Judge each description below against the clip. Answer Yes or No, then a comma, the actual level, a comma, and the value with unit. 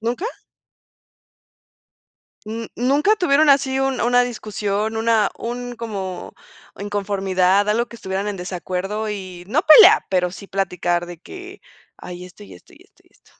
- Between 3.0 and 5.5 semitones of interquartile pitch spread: Yes, average, 4.7 semitones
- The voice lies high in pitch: Yes, high, 210 Hz